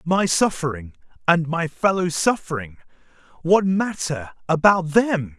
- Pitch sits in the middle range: Yes, medium, 165 Hz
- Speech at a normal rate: No, slow, 100 wpm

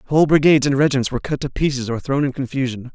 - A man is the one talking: Yes, male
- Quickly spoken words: Yes, fast, 245 wpm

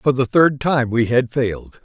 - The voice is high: No, low, 125 Hz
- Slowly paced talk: No, fast, 230 wpm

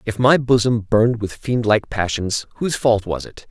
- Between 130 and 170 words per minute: No, fast, 205 wpm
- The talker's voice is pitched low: Yes, low, 110 Hz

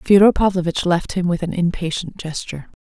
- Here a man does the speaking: No, female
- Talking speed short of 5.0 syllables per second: No, 5.6 syllables/s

